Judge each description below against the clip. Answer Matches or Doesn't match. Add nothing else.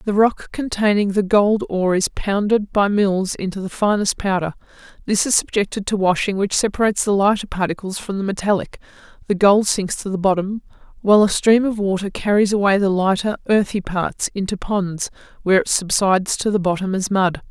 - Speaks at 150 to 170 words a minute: Doesn't match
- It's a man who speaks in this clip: Doesn't match